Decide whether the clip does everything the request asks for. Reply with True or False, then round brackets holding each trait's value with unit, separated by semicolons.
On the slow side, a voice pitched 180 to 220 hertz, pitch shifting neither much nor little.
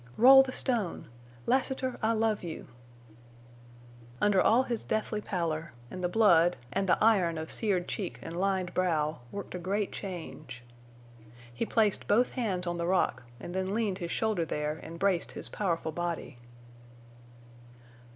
False (150 wpm; 185 Hz; 4.3 semitones)